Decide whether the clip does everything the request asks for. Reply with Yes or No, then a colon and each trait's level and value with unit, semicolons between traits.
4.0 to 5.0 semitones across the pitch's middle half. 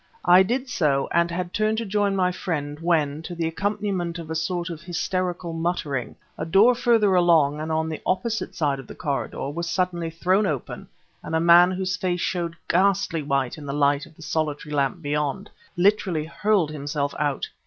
No: average, 3.5 semitones